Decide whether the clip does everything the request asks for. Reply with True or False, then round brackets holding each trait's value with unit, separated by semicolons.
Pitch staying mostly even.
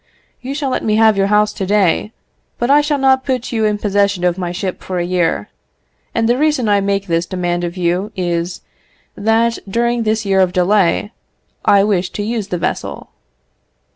False (4.0 semitones)